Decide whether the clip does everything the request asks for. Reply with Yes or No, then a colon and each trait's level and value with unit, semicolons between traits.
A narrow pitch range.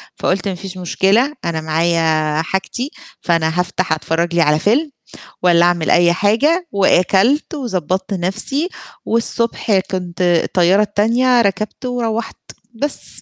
No: average, 5.2 semitones